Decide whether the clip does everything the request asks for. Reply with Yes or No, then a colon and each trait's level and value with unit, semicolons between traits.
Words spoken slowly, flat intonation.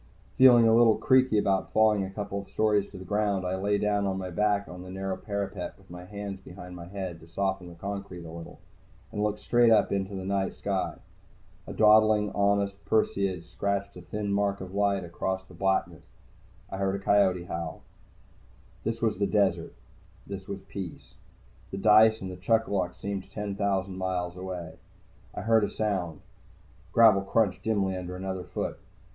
No: average, 180 wpm; narrow, 1.8 semitones